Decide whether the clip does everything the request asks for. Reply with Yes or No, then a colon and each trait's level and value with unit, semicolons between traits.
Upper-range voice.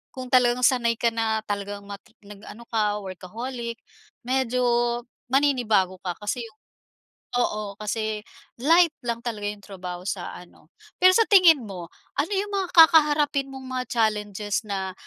Yes: high, 230 Hz